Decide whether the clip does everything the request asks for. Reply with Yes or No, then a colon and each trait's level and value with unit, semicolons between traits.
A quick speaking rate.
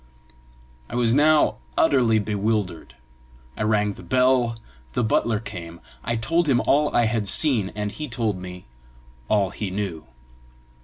No: average, 145 wpm